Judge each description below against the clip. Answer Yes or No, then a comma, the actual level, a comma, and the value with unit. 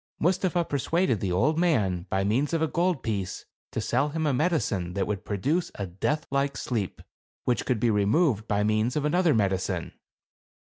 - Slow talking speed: No, average, 180 wpm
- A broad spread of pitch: Yes, wide, 7.8 semitones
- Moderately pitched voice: No, low, 125 Hz